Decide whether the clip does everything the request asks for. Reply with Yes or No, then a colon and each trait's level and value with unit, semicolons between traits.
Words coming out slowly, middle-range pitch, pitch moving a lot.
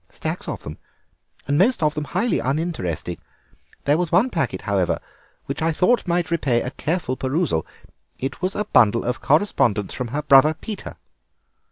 No: average, 165 wpm; medium, 150 Hz; wide, 5.9 semitones